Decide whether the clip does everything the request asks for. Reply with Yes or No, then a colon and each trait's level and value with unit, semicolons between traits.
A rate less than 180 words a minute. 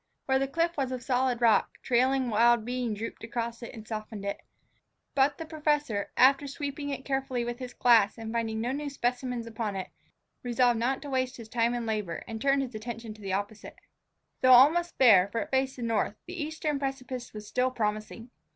No: average, 190 wpm